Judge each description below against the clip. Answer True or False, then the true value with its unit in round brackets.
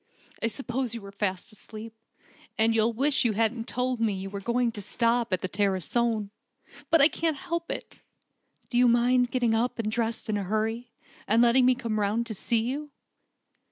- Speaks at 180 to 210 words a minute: True (190 wpm)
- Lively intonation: False (2.6 semitones)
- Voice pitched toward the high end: True (230 Hz)